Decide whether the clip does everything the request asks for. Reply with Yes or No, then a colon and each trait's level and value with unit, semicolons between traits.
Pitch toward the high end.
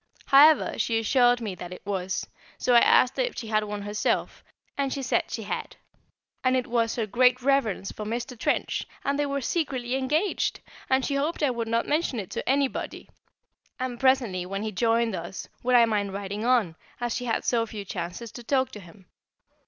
Yes: high, 235 Hz